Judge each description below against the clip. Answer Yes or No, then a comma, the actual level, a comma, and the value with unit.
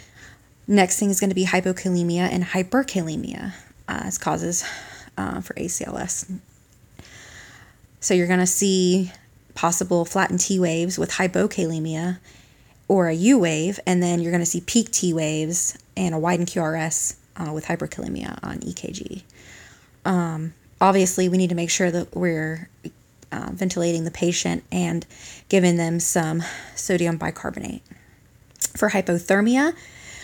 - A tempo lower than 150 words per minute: Yes, slow, 135 wpm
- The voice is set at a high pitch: No, medium, 175 Hz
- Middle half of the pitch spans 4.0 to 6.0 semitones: No, narrow, 2.5 semitones